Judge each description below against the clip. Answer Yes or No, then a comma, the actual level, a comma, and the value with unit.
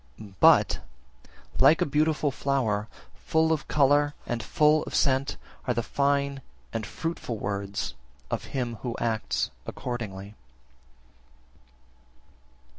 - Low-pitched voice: Yes, low, 130 Hz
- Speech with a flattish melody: No, average, 4.8 semitones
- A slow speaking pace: Yes, slow, 115 wpm